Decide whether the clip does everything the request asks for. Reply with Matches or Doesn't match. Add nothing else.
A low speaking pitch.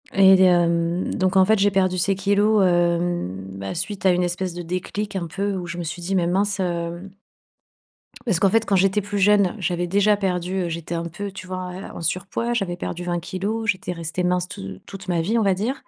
Doesn't match